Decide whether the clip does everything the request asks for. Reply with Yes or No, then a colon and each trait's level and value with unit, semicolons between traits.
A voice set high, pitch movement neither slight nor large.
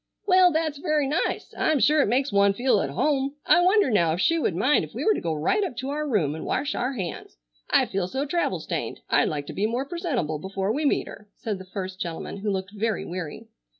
No: high, 240 Hz; wide, 7.8 semitones